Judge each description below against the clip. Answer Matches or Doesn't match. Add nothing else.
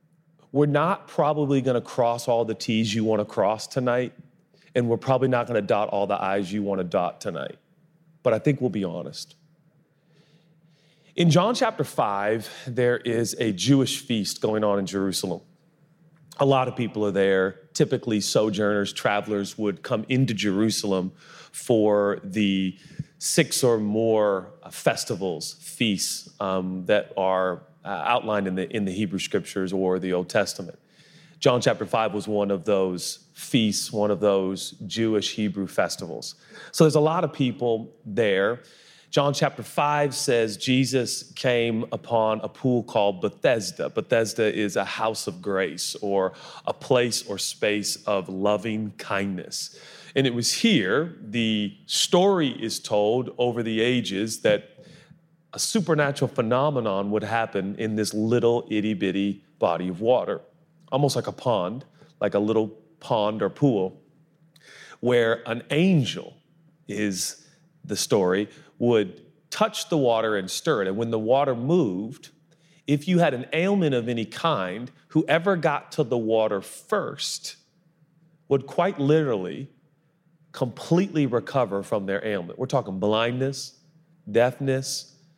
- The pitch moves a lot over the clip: Matches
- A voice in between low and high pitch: Doesn't match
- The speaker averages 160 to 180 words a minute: Doesn't match